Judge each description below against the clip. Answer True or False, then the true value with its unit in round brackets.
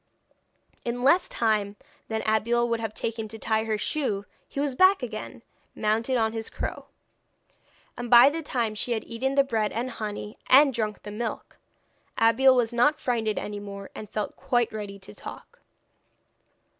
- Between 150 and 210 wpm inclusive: True (170 wpm)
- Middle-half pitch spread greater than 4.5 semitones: False (2.6 semitones)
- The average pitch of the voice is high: True (230 Hz)